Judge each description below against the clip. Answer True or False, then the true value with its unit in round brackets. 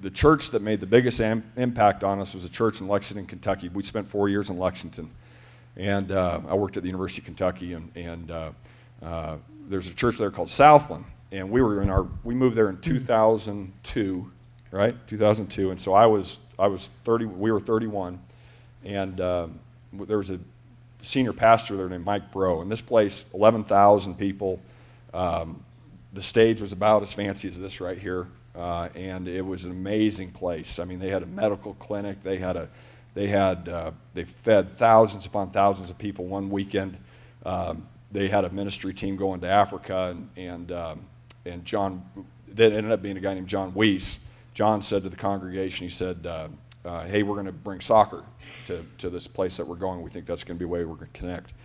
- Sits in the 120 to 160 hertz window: False (100 Hz)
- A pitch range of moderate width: True (3.1 semitones)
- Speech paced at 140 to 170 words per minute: False (205 wpm)